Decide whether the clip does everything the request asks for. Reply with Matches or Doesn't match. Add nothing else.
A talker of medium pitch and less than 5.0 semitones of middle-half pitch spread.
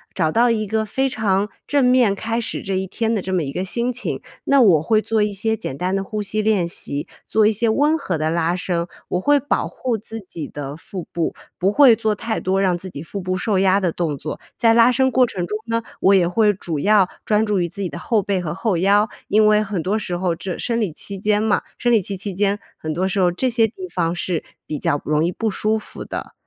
Doesn't match